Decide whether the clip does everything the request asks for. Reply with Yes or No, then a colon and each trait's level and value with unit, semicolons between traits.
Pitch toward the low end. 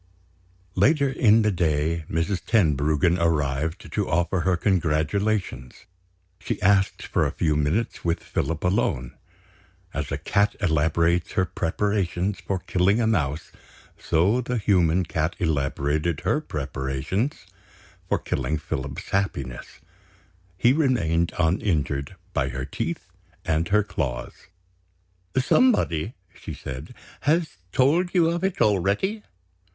Yes: very low, 85 Hz